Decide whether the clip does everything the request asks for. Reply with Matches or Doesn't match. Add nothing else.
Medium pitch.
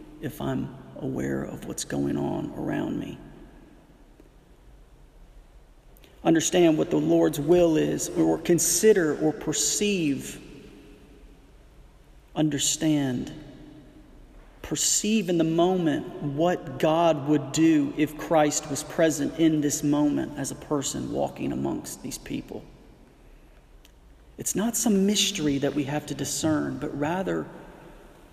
Matches